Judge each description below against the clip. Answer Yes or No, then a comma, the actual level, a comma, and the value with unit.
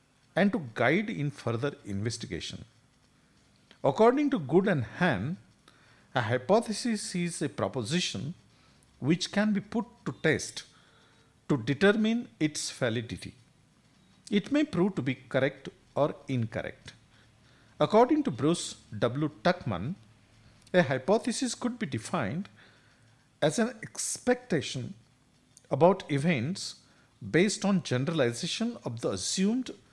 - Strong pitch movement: Yes, wide, 8.4 semitones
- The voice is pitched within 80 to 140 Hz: No, medium, 150 Hz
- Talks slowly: Yes, slow, 110 wpm